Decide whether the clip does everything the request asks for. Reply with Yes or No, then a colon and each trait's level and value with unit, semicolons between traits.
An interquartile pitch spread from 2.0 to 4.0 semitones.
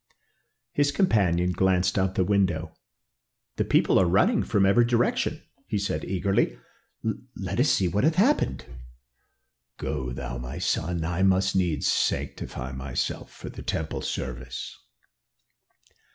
No: average, 4.5 semitones